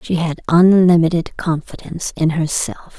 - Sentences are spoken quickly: No, slow, 120 wpm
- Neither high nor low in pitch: Yes, medium, 165 Hz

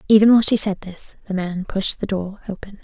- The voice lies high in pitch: Yes, high, 200 Hz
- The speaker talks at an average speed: No, fast, 230 wpm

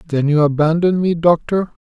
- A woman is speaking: No, male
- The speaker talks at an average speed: Yes, average, 165 wpm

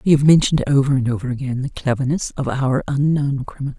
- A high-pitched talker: No, low, 135 Hz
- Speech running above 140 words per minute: Yes, fast, 205 wpm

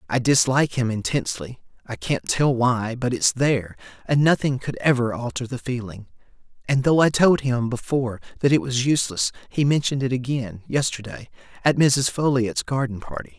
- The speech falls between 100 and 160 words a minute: Yes, average, 145 wpm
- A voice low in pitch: Yes, low, 130 Hz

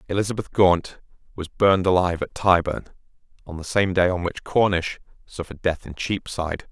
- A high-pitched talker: No, very low, 90 Hz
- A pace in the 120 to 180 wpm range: Yes, average, 160 wpm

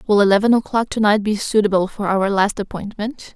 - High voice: Yes, high, 205 Hz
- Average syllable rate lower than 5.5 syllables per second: No, 5.6 syllables/s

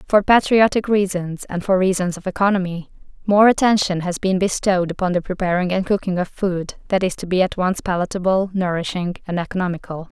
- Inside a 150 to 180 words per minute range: Yes, average, 175 wpm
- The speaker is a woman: Yes, female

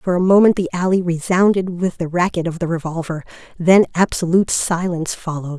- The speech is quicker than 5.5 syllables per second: Yes, 5.9 syllables/s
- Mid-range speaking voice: Yes, medium, 175 Hz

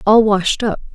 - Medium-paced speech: Yes, average, 190 wpm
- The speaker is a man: No, female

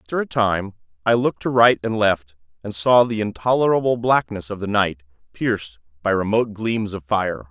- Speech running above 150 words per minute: Yes, average, 185 wpm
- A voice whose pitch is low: Yes, low, 105 Hz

